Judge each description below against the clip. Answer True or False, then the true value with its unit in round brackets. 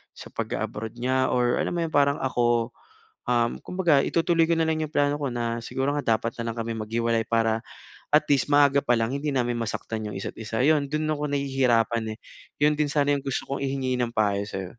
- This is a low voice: True (130 Hz)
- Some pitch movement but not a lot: True (3.9 semitones)